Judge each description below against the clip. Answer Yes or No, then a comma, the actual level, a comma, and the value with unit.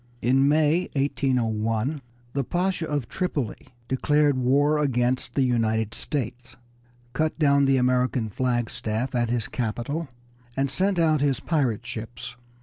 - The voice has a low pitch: Yes, low, 130 Hz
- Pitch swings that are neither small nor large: Yes, average, 3.5 semitones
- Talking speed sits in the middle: No, slow, 130 wpm